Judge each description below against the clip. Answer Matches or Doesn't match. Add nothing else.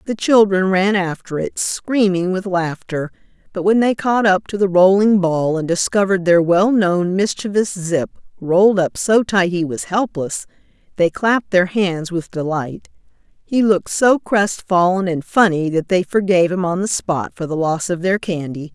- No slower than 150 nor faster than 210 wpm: Matches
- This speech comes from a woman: Matches